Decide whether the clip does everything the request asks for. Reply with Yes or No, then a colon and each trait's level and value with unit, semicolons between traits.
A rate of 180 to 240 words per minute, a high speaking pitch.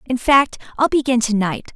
Yes: fast, 205 wpm; very high, 250 Hz